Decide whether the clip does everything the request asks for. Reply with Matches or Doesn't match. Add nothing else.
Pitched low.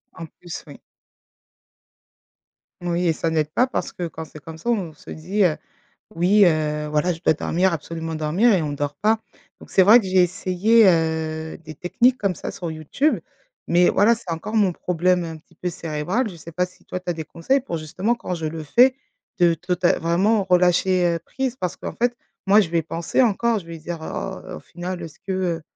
Doesn't match